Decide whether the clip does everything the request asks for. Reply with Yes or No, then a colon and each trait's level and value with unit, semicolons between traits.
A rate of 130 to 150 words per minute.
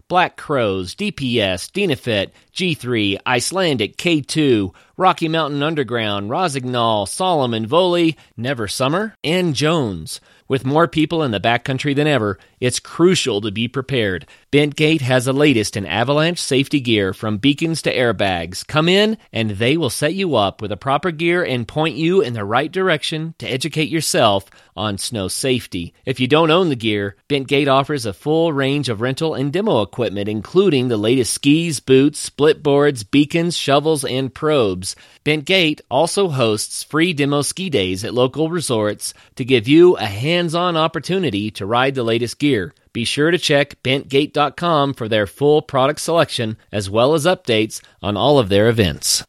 No: average, 165 wpm